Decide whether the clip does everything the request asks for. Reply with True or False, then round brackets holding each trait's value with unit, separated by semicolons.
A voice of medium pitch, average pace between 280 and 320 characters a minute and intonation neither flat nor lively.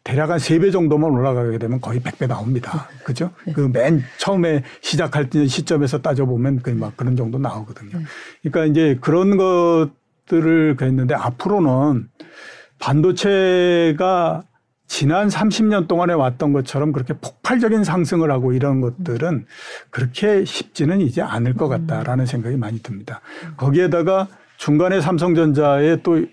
True (150 Hz; 315 characters per minute; 4.9 semitones)